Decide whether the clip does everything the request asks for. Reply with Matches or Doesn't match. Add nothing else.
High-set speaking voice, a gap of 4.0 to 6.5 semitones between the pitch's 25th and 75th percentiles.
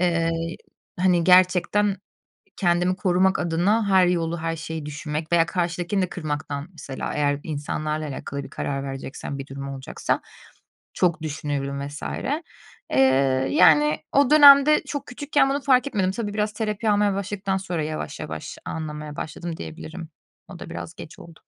Doesn't match